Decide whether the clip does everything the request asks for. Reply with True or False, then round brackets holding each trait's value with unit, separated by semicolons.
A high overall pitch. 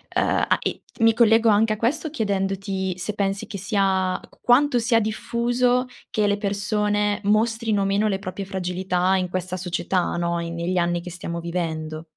True (195 Hz)